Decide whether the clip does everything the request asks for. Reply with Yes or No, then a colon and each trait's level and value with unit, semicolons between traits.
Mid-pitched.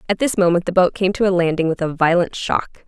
Yes: medium, 180 Hz